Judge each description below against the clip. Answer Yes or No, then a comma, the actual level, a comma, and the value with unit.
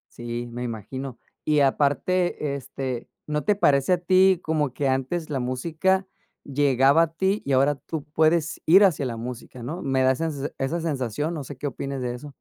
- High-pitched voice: No, medium, 140 Hz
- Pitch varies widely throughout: No, average, 4.0 semitones